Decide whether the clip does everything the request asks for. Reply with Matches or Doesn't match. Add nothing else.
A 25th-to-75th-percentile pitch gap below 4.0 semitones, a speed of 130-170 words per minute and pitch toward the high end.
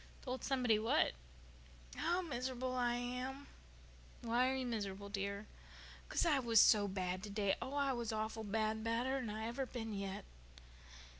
Matches